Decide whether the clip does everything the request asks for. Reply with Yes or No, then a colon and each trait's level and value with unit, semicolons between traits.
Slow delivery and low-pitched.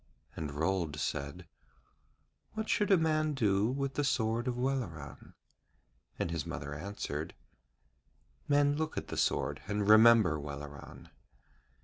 Yes: slow, 125 wpm; low, 105 Hz